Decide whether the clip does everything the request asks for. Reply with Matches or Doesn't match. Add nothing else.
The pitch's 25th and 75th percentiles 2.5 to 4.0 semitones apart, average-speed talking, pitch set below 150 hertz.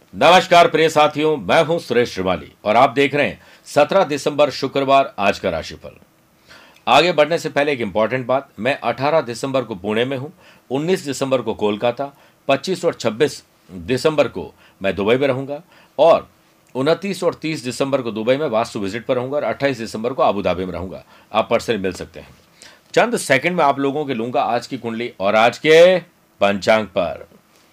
Doesn't match